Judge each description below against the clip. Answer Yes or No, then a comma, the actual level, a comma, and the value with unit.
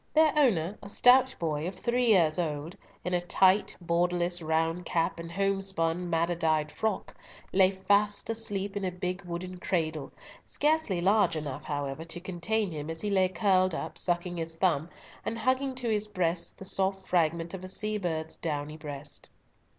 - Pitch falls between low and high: Yes, medium, 180 Hz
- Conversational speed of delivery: Yes, average, 175 wpm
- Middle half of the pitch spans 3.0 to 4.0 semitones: Yes, average, 3.4 semitones